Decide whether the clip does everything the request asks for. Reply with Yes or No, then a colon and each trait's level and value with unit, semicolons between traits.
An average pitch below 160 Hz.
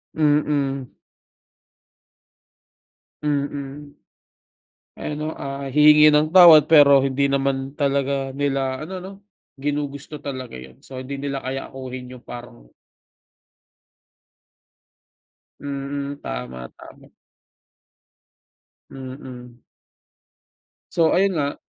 Yes: medium, 140 Hz